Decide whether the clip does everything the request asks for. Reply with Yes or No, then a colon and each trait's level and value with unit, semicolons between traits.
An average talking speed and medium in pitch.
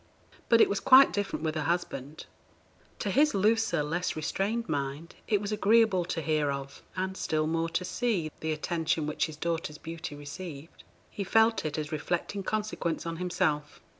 Yes: average, 170 wpm; medium, 170 Hz